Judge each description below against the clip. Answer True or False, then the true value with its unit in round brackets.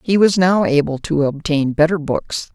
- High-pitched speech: False (160 Hz)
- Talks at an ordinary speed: True (190 wpm)